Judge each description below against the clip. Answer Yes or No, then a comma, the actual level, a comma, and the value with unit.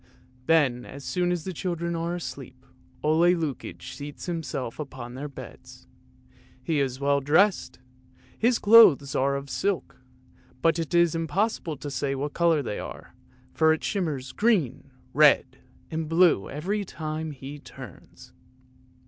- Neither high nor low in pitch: Yes, medium, 155 Hz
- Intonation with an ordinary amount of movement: Yes, average, 3.8 semitones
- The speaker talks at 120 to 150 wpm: Yes, average, 145 wpm